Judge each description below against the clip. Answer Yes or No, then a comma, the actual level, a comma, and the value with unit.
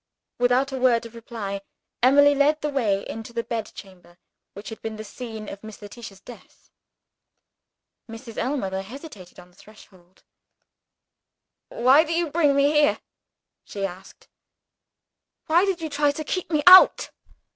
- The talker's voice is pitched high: Yes, high, 235 Hz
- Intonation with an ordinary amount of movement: No, wide, 5.9 semitones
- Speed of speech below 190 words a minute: Yes, average, 150 wpm